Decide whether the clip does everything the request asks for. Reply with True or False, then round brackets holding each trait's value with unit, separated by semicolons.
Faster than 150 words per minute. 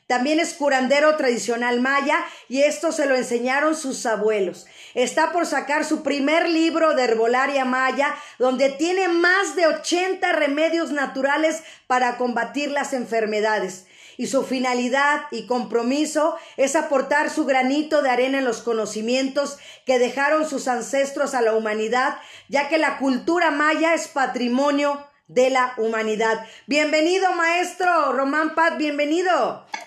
False (135 wpm)